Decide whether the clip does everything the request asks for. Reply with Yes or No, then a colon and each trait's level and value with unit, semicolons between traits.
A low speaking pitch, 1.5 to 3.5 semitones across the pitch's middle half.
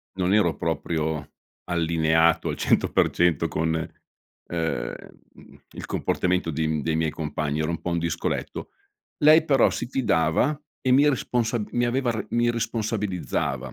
No: very low, 85 Hz; wide, 6.7 semitones